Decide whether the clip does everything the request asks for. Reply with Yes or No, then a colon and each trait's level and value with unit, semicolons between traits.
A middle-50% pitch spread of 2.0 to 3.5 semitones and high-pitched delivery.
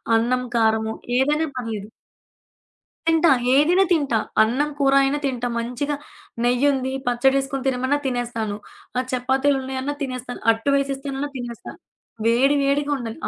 Yes: narrow, 2.6 semitones; very high, 265 Hz